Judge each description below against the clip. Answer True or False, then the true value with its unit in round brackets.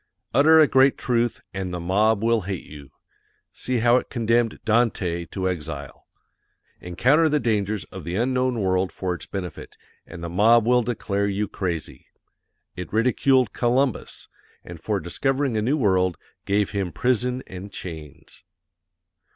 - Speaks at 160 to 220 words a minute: False (150 wpm)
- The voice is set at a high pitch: False (105 Hz)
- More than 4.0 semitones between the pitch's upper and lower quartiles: True (5.1 semitones)